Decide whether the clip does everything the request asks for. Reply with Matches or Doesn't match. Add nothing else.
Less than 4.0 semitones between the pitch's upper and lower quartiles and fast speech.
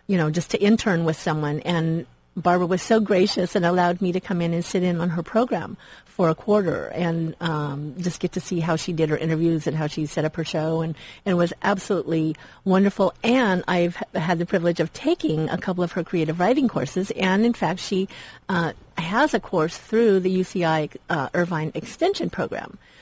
Matches